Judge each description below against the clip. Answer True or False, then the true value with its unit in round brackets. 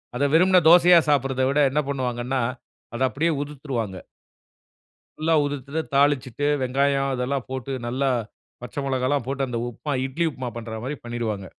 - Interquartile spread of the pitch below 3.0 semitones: True (2.5 semitones)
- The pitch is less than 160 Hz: True (135 Hz)